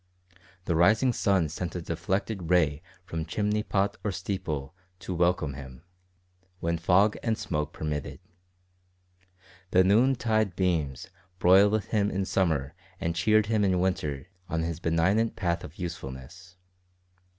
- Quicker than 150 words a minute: No, slow, 135 wpm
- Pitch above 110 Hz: No, very low, 90 Hz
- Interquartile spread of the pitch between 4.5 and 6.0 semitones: No, average, 3.8 semitones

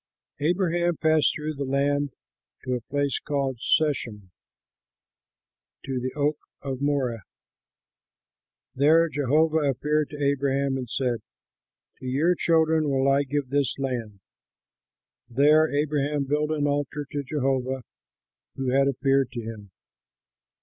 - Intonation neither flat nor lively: No, narrow, 2.2 semitones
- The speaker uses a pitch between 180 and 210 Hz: No, medium, 140 Hz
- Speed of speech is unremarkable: No, slow, 120 wpm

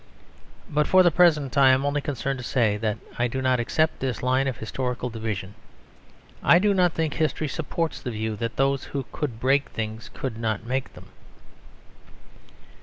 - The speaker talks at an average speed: Yes, average, 180 wpm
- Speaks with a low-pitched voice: Yes, low, 130 Hz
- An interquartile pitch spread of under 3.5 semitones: No, average, 4.2 semitones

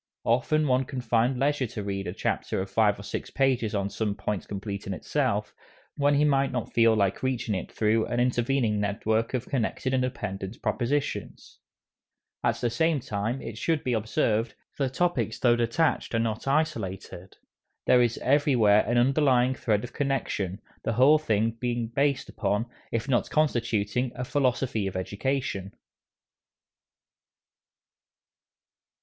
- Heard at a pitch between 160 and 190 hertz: No, low, 120 Hz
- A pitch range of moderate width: Yes, average, 4.1 semitones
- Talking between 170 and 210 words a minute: No, average, 150 wpm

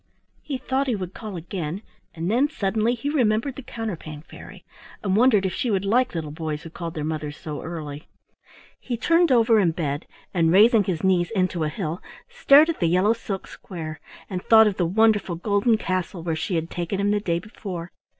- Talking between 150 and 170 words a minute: No, average, 200 wpm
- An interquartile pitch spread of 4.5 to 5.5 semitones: Yes, average, 5.2 semitones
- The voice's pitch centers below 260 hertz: Yes, high, 190 Hz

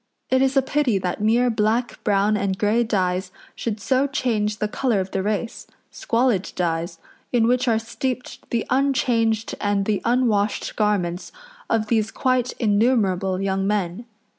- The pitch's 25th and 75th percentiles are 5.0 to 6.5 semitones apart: No, average, 3.7 semitones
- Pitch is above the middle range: Yes, high, 215 Hz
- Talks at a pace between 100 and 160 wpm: Yes, average, 155 wpm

